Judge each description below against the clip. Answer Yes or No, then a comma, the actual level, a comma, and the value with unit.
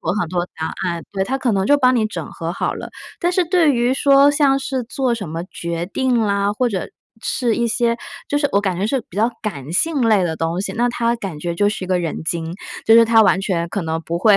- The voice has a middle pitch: No, high, 210 Hz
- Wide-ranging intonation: Yes, wide, 6.3 semitones